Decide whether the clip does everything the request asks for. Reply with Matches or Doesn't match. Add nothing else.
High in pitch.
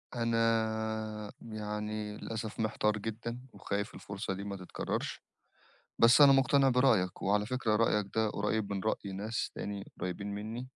Doesn't match